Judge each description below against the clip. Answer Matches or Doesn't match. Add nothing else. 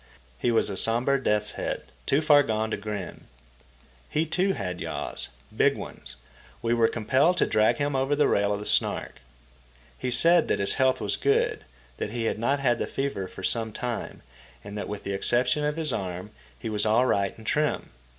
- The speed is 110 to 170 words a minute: Doesn't match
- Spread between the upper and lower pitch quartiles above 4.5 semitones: Matches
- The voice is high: Doesn't match